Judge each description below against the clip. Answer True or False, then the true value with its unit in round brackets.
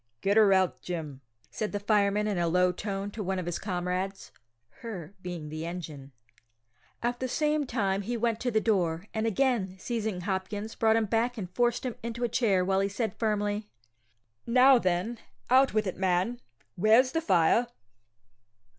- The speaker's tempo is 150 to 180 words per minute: True (175 wpm)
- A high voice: True (205 Hz)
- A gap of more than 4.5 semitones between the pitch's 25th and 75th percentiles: False (4.1 semitones)